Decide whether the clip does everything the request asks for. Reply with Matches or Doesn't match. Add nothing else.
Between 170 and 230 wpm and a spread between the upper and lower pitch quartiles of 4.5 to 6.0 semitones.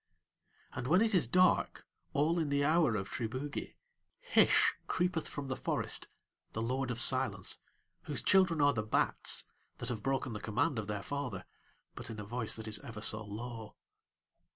Matches